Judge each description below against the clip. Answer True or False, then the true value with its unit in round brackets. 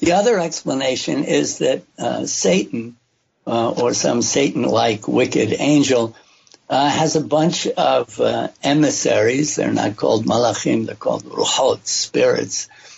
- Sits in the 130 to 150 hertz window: True (140 Hz)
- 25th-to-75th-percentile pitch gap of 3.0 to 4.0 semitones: False (5.0 semitones)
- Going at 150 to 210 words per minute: False (135 wpm)